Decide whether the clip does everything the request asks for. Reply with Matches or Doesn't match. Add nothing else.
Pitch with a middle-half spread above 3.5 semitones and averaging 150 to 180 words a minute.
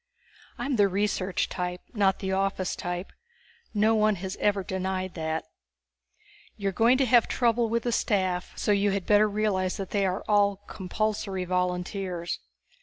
Doesn't match